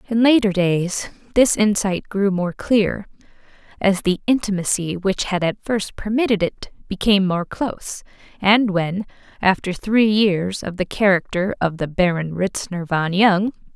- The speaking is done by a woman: Yes, female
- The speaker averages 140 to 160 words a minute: Yes, average, 150 wpm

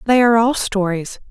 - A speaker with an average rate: Yes, average, 185 wpm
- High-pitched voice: Yes, high, 215 Hz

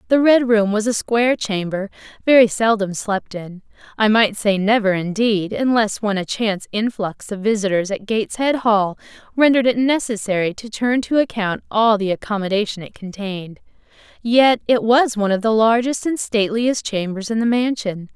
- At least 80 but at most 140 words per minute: No, average, 170 wpm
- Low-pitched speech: No, high, 215 Hz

